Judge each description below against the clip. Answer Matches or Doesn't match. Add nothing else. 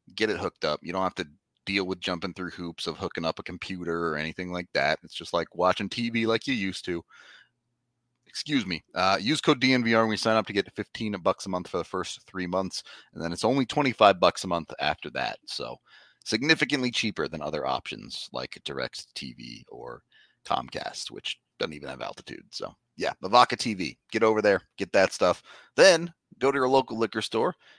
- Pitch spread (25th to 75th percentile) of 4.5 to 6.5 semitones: Matches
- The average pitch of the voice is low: Matches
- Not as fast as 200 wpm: Doesn't match